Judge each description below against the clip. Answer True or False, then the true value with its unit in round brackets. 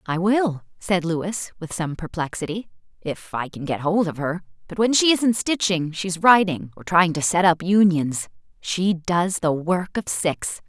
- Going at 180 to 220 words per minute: True (185 wpm)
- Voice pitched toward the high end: False (180 Hz)